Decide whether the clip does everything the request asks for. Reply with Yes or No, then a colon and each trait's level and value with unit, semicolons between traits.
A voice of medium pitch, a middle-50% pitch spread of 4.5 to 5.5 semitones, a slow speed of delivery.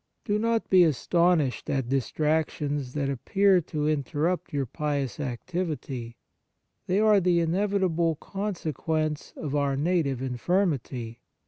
Yes: medium, 155 Hz; average, 4.8 semitones; slow, 130 wpm